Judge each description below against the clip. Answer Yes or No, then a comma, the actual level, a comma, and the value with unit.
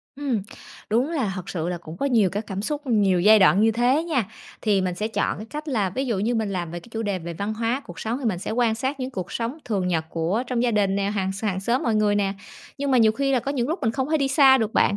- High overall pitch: Yes, high, 220 Hz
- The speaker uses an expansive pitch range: No, average, 4.7 semitones